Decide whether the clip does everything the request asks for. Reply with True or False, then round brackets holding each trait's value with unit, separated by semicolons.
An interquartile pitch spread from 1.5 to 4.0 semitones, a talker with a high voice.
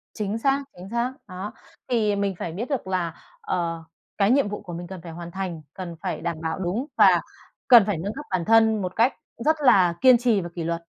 False (4.6 semitones; 195 Hz)